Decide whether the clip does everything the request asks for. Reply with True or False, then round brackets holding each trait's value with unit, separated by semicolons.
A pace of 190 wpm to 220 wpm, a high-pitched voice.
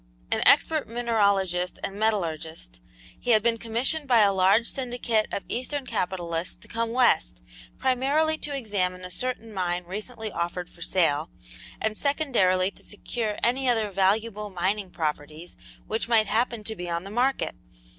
False (155 wpm; 215 Hz)